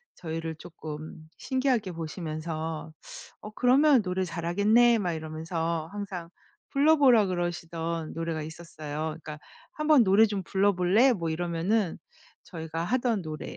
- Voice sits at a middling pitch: Yes, medium, 175 Hz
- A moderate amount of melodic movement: Yes, average, 4.8 semitones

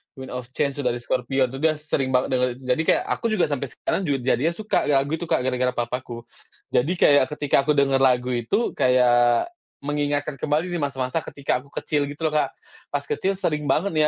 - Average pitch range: Yes, average, 3.0 semitones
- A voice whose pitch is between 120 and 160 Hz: Yes, medium, 140 Hz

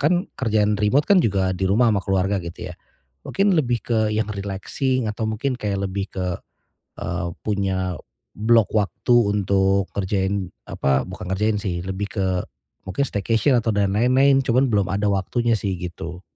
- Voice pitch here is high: No, low, 100 Hz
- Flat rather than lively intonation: No, average, 3.5 semitones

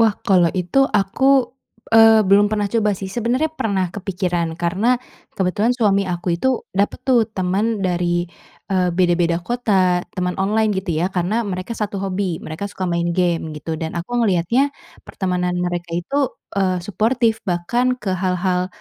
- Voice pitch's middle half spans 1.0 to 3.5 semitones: No, average, 3.9 semitones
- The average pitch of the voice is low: No, high, 190 Hz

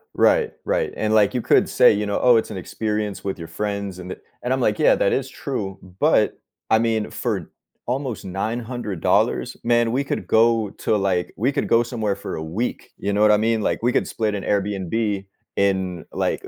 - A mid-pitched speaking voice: No, low, 105 Hz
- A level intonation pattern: No, average, 3.1 semitones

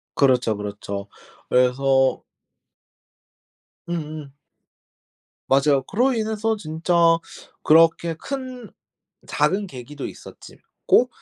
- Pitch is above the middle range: No, medium, 155 Hz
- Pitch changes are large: Yes, wide, 7.4 semitones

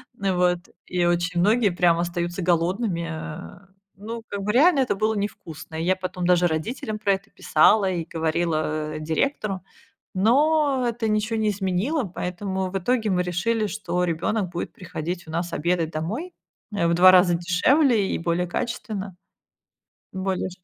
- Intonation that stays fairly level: No, average, 3.7 semitones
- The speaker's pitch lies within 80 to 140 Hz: No, medium, 185 Hz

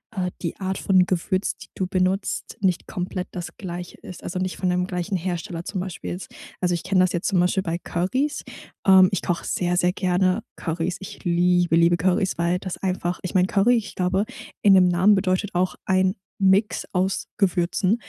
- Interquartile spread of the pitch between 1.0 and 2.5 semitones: Yes, narrow, 1.4 semitones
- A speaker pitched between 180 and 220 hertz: Yes, medium, 185 Hz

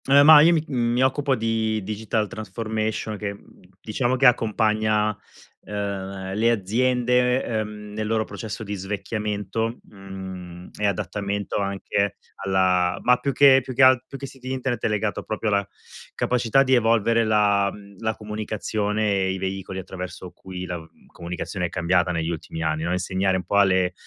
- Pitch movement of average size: Yes, average, 3.3 semitones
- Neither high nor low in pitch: No, low, 105 Hz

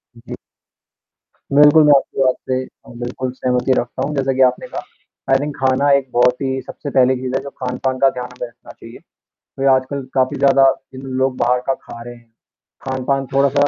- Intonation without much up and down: Yes, narrow, 1.5 semitones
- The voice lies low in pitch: Yes, low, 130 Hz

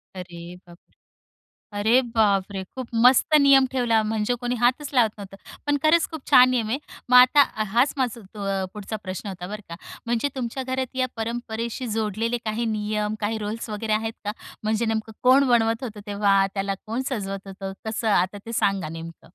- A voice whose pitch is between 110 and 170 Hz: No, high, 220 Hz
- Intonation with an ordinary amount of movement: Yes, average, 3.4 semitones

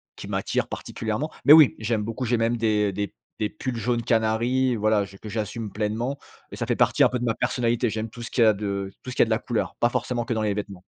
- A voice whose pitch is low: Yes, low, 115 Hz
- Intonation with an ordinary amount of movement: No, narrow, 2.2 semitones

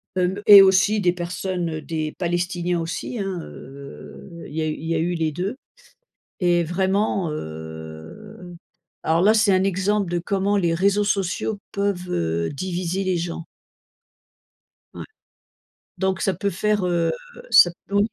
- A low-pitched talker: No, medium, 180 Hz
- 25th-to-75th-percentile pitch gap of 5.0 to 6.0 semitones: No, average, 2.8 semitones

